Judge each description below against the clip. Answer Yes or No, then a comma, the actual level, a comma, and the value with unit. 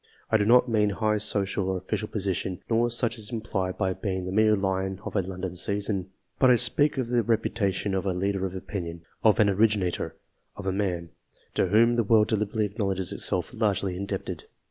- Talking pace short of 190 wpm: No, average, 200 wpm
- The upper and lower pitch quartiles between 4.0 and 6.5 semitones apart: No, average, 2.7 semitones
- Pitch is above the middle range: No, low, 100 Hz